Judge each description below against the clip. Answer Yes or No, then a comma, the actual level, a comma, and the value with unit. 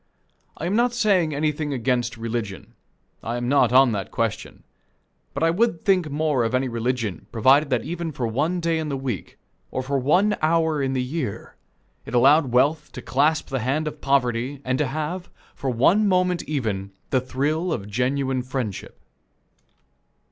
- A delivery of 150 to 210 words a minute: Yes, average, 170 wpm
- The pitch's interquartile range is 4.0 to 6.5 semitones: Yes, average, 4.3 semitones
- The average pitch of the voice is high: No, medium, 140 Hz